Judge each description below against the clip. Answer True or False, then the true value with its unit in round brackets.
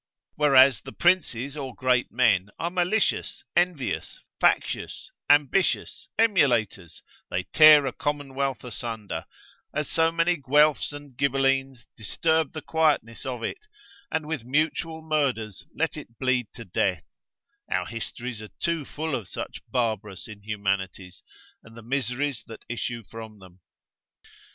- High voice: False (130 Hz)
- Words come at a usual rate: False (130 wpm)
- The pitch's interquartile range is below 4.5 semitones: False (5.2 semitones)